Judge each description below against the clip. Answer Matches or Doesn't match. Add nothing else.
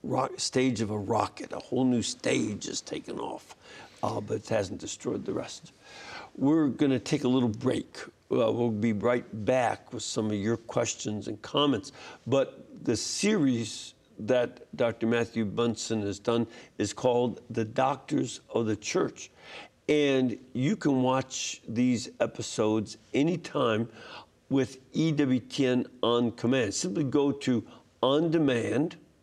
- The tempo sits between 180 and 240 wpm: Doesn't match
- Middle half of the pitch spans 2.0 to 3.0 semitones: Matches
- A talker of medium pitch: Doesn't match